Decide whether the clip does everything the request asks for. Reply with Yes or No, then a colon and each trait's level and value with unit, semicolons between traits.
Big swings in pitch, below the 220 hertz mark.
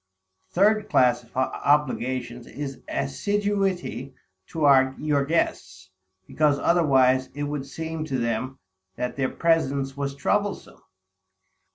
No: average, 3.8 semitones; medium, 140 Hz